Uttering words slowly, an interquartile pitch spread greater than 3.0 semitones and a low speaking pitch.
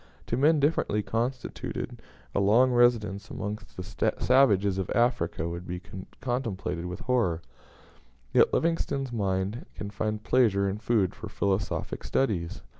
Yes: slow, 130 wpm; average, 4.4 semitones; low, 105 Hz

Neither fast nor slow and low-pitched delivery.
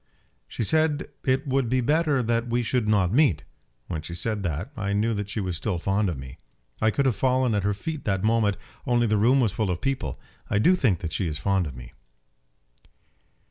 No: fast, 220 wpm; low, 110 Hz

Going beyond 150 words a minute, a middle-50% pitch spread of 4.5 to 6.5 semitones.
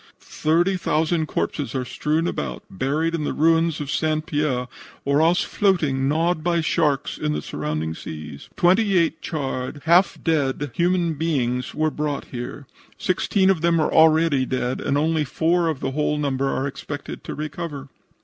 No: average, 165 wpm; average, 3.6 semitones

